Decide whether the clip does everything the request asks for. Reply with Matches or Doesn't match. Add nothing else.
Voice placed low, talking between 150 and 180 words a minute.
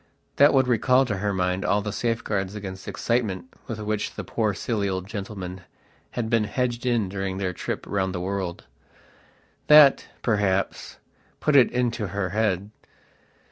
Matches